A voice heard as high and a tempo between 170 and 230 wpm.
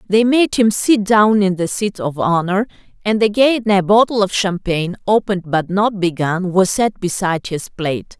Yes: high, 195 Hz; average, 185 wpm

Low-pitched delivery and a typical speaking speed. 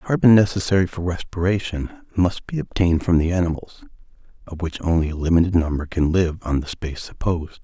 Yes: very low, 90 Hz; average, 180 wpm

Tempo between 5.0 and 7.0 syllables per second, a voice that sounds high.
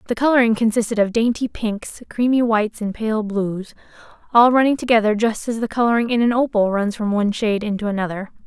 Yes: 6.0 syllables/s; high, 220 Hz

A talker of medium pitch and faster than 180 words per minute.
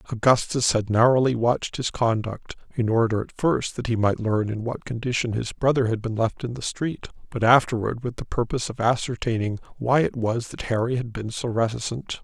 No: low, 120 Hz; average, 200 wpm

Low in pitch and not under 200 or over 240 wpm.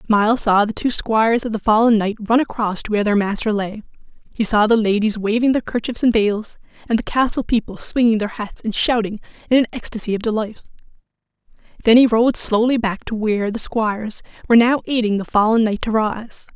No: high, 220 Hz; fast, 205 wpm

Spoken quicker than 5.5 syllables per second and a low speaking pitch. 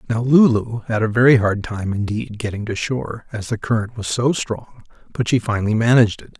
Yes: 5.7 syllables/s; low, 110 Hz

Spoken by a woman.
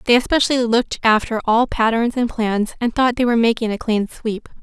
Yes: female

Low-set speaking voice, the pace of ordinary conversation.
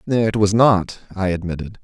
Yes: low, 100 Hz; average, 165 wpm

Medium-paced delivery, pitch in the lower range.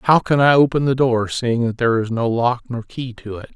No: fast, 270 wpm; low, 120 Hz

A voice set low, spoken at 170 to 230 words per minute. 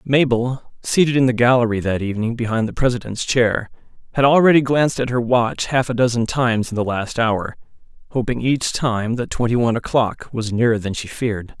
Yes: low, 120 Hz; average, 190 wpm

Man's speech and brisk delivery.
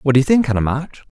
Yes: male; fast, 320 wpm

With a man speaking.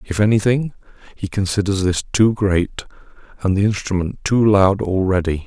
Yes: male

